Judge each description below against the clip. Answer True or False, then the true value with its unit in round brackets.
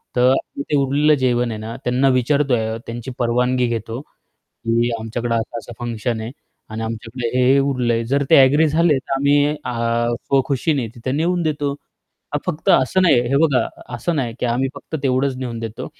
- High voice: False (125 Hz)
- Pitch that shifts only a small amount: False (3.1 semitones)